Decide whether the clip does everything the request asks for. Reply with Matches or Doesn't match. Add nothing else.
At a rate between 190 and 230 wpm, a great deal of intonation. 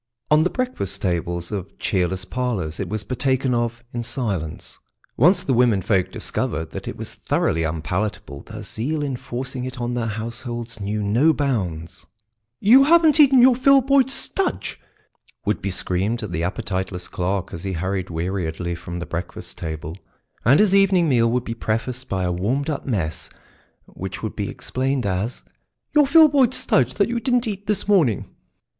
Doesn't match